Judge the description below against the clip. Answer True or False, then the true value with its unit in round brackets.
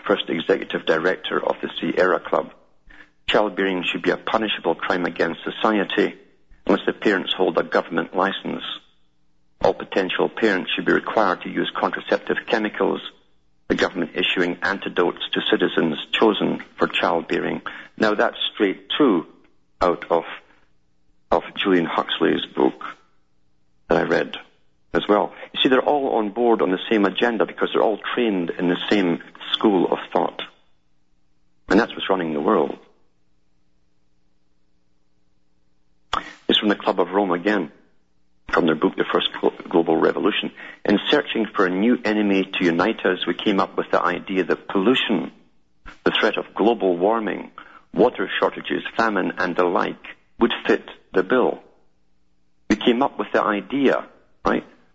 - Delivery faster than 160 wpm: False (145 wpm)